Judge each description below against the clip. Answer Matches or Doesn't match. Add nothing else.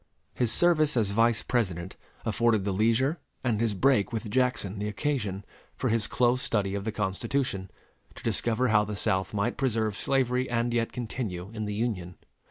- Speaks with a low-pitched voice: Matches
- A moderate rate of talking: Matches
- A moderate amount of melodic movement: Matches